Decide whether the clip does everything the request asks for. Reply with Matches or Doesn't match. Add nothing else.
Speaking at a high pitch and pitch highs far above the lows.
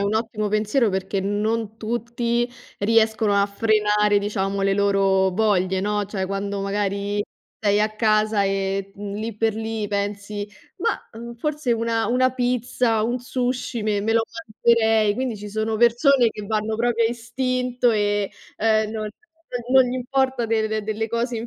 Doesn't match